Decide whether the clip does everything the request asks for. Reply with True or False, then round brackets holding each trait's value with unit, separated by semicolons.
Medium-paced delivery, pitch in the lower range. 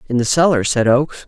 False (235 wpm; 130 Hz)